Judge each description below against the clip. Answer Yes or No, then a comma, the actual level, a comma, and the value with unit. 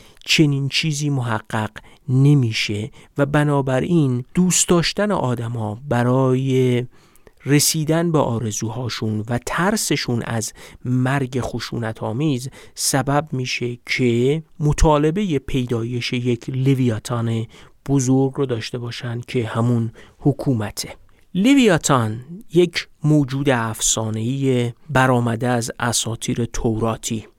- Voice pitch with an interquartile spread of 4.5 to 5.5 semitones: No, average, 3.7 semitones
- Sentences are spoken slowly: Yes, slow, 90 wpm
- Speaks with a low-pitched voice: Yes, low, 130 Hz